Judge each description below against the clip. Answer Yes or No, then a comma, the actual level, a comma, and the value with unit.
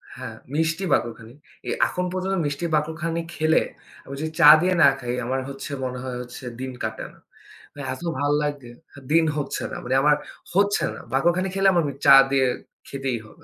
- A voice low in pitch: No, medium, 145 Hz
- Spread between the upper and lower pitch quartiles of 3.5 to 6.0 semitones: Yes, average, 4.2 semitones